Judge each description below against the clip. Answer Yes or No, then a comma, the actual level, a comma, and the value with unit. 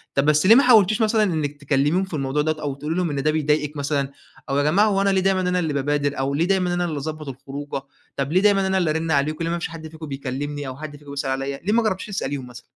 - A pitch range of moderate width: Yes, average, 4.3 semitones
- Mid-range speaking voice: Yes, medium, 155 Hz